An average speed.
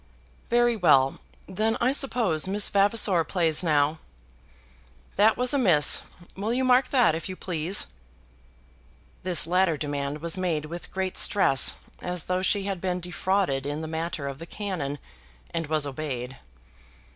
Yes: average, 150 wpm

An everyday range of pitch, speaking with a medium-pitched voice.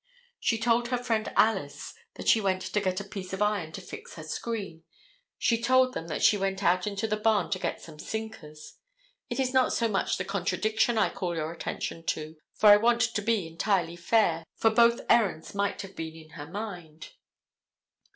No: average, 4.9 semitones; high, 200 Hz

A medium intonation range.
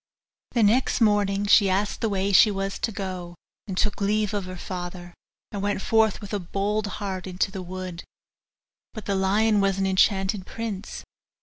No: narrow, 1.9 semitones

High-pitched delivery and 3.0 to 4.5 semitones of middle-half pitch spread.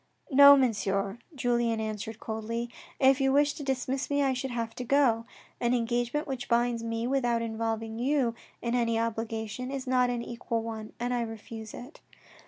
No: high, 235 Hz; narrow, 2.4 semitones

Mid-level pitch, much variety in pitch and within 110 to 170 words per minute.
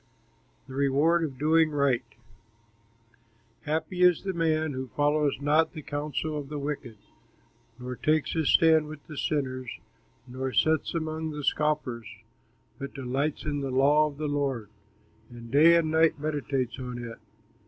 No: medium, 145 Hz; average, 2.9 semitones; average, 145 wpm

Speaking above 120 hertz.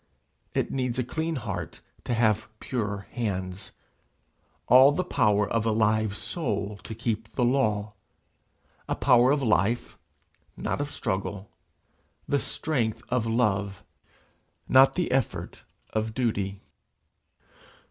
No: low, 110 Hz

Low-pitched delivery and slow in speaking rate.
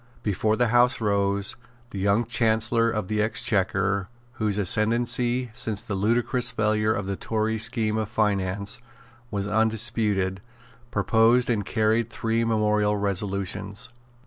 Yes: low, 110 Hz; slow, 125 wpm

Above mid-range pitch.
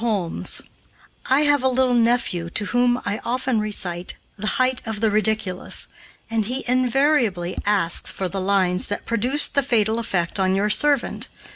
Yes: high, 220 Hz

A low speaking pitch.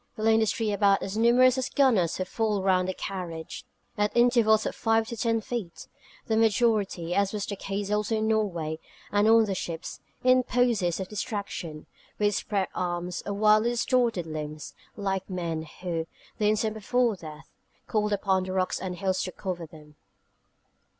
No: high, 205 Hz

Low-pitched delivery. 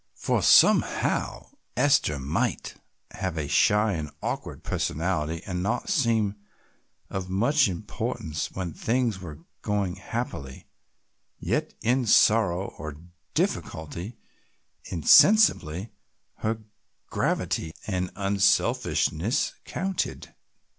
Yes: very low, 95 Hz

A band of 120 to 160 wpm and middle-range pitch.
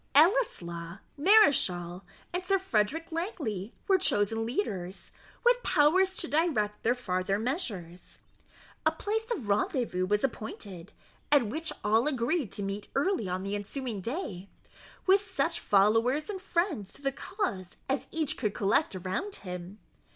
No: average, 140 wpm; high, 240 Hz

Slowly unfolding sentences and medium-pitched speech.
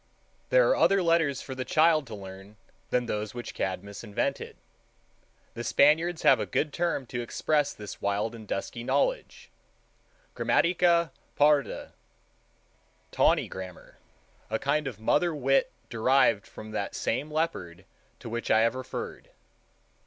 No: slow, 130 wpm; low, 130 Hz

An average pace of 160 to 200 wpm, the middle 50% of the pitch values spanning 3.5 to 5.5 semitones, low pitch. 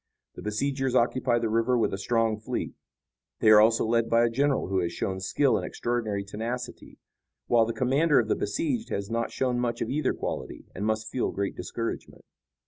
No: average, 195 wpm; average, 2.7 semitones; low, 115 Hz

